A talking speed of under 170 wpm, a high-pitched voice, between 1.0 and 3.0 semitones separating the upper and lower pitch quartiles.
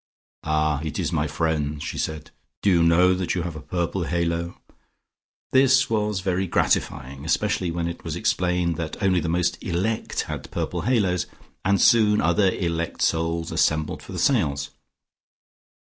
No: average, 160 wpm; very low, 85 Hz; average, 2.7 semitones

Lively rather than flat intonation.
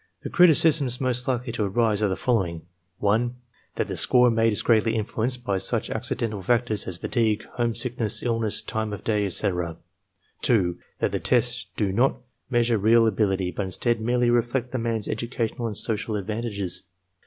No: average, 2.8 semitones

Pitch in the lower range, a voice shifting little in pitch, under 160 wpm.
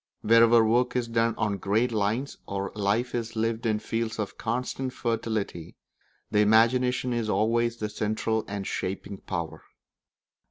Yes: low, 110 Hz; narrow, 2.0 semitones; average, 145 wpm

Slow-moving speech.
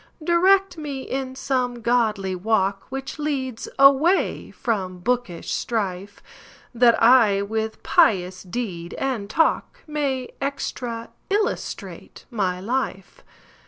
Yes: slow, 90 wpm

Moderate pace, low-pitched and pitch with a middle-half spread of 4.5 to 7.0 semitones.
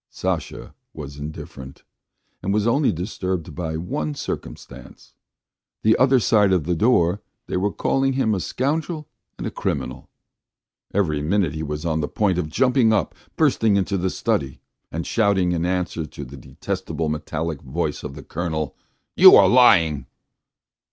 Yes: average, 155 wpm; very low, 90 Hz; average, 5.1 semitones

